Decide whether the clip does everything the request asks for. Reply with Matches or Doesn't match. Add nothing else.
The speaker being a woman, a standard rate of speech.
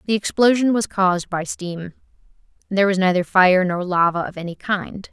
Matches